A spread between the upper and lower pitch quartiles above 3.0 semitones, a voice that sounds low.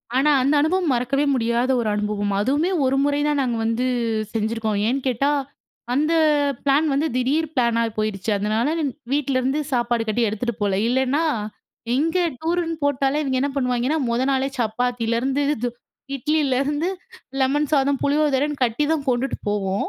No: average, 3.7 semitones; very high, 265 Hz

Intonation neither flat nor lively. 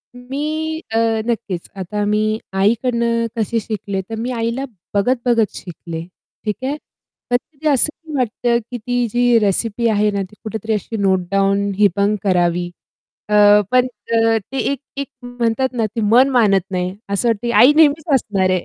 Yes: average, 3.7 semitones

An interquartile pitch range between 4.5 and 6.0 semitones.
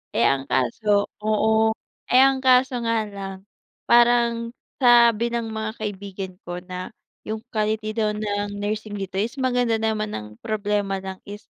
No: narrow, 2.4 semitones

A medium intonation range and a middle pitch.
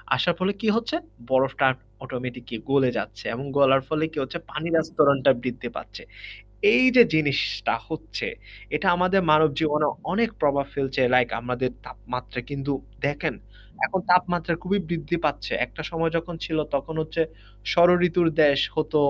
Yes: average, 4.3 semitones; medium, 150 Hz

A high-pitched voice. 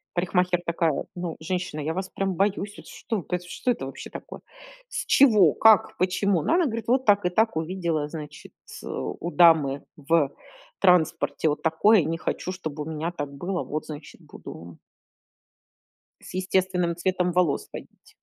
No: medium, 175 Hz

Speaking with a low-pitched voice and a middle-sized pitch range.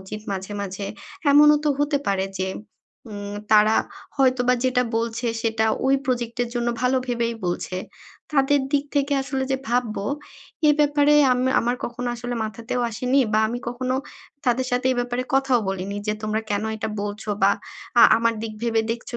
No: high, 240 Hz; average, 3.1 semitones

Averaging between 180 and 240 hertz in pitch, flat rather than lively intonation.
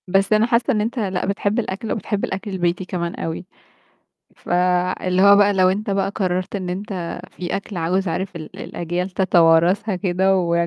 Yes: high, 190 Hz; narrow, 2.1 semitones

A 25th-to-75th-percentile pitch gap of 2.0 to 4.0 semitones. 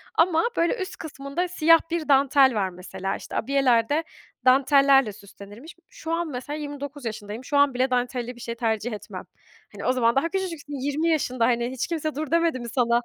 No: average, 4.6 semitones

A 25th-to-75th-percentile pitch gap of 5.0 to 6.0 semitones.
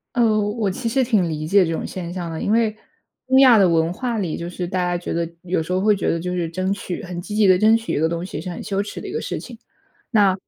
No: average, 3.7 semitones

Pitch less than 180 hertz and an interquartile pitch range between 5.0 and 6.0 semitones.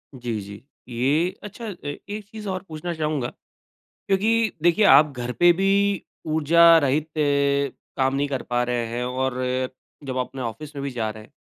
Yes: medium, 140 Hz; wide, 5.5 semitones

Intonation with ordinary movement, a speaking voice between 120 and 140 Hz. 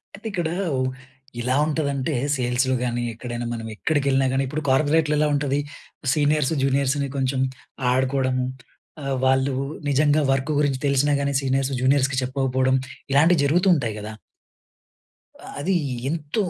No: narrow, 2.1 semitones; low, 135 Hz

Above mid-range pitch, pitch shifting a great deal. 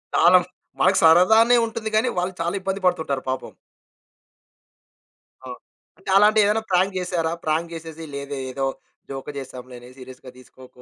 No: medium, 165 Hz; wide, 6.1 semitones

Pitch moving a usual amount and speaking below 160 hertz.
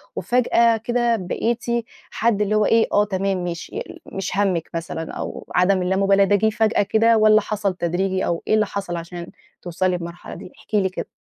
No: average, 3.3 semitones; high, 195 Hz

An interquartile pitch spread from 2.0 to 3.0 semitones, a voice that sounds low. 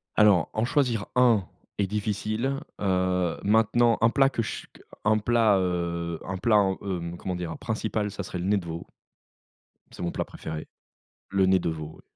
No: average, 3.9 semitones; low, 100 Hz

